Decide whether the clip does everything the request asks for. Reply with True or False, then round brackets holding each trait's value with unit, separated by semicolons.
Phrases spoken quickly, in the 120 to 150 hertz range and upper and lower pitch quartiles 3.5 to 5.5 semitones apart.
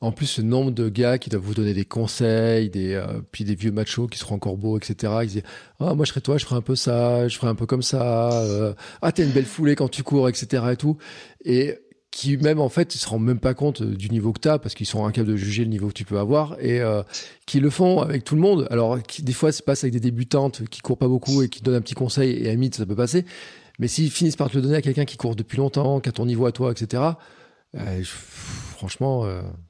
True (285 wpm; 125 Hz; 3.8 semitones)